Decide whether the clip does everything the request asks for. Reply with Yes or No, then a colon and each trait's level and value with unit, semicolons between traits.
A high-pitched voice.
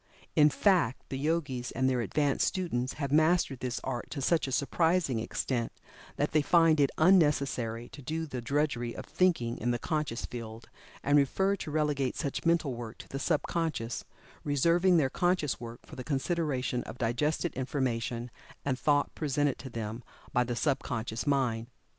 No: medium, 140 Hz